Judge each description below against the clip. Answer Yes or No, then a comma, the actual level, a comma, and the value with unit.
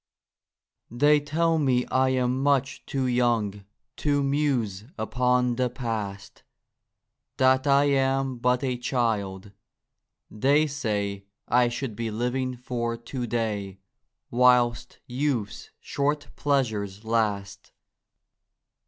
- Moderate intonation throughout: Yes, average, 3.4 semitones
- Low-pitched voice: Yes, low, 125 Hz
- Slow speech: Yes, slow, 110 wpm